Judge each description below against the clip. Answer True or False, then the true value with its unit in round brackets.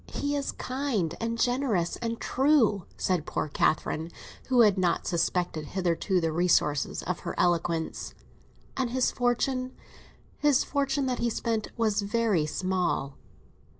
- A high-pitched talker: True (210 Hz)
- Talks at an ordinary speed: False (125 wpm)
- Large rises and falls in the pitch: True (6.5 semitones)